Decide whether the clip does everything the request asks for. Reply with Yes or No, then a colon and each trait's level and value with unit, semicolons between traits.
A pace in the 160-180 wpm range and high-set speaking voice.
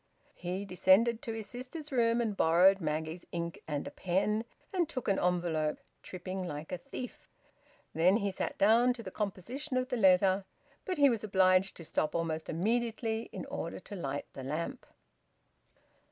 Yes: average, 170 wpm; high, 195 Hz